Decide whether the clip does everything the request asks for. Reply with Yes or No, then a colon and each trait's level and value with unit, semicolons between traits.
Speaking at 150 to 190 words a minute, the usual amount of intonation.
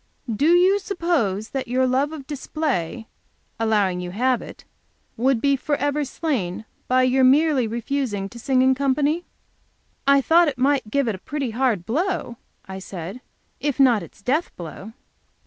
Yes: average, 160 wpm; average, 4.6 semitones